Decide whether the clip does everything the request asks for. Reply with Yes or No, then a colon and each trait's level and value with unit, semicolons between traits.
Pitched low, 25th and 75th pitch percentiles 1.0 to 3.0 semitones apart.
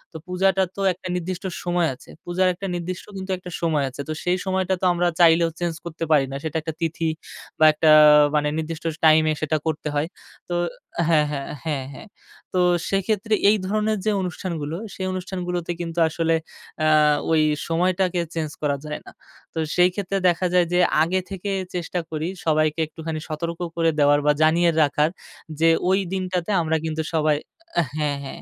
No: medium, 170 Hz; average, 2.7 semitones